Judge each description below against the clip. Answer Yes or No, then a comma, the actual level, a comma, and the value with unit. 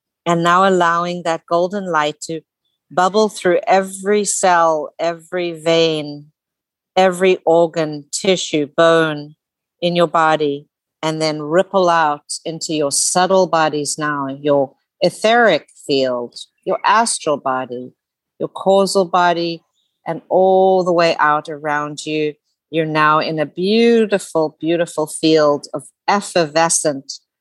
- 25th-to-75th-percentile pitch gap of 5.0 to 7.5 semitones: No, average, 3.3 semitones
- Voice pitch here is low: No, medium, 165 Hz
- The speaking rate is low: Yes, slow, 120 wpm